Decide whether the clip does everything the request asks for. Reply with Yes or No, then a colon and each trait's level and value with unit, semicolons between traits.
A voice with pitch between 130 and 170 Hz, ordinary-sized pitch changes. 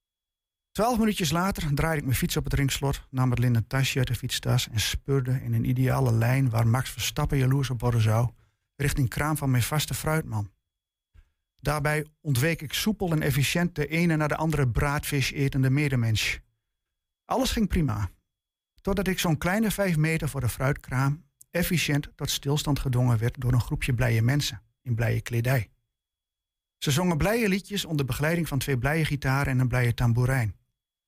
Yes: low, 135 Hz; average, 4.4 semitones